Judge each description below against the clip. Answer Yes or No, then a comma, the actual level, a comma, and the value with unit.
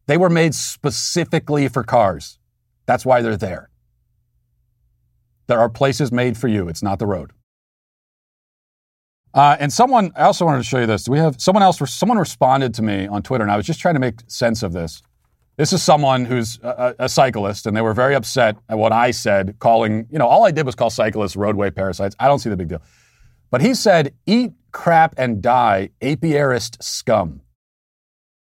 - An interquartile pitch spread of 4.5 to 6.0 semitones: Yes, average, 5.2 semitones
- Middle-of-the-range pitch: No, low, 120 Hz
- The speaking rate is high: No, average, 195 wpm